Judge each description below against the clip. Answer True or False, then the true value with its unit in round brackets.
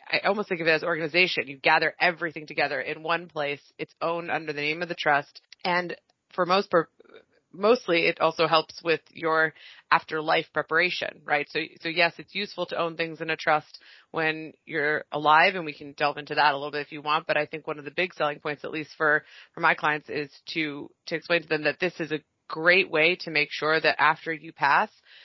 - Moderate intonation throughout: False (2.1 semitones)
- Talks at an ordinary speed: False (225 wpm)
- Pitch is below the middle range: False (160 Hz)